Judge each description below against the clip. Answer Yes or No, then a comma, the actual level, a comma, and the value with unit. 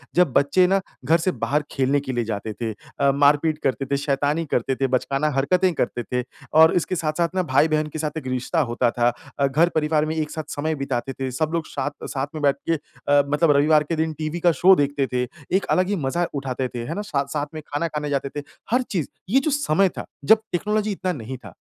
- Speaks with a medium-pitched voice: Yes, medium, 150 Hz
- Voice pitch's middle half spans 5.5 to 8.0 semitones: No, average, 3.3 semitones